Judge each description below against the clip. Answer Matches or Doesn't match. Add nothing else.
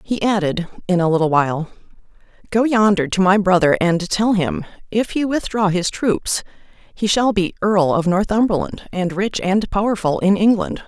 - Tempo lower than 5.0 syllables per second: Matches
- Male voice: Doesn't match